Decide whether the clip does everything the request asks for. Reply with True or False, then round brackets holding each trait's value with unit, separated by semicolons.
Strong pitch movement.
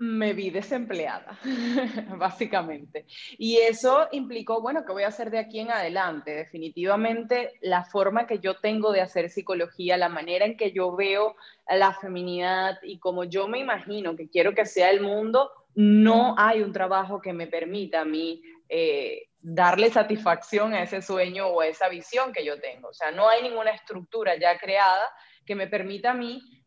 False (3.9 semitones)